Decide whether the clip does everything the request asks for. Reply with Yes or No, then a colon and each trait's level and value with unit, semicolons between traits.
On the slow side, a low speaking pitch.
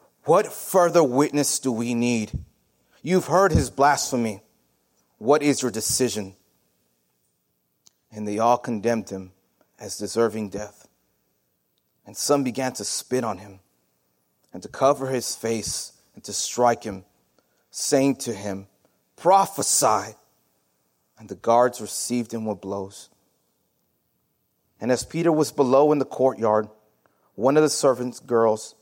Yes: slow, 130 wpm; low, 115 Hz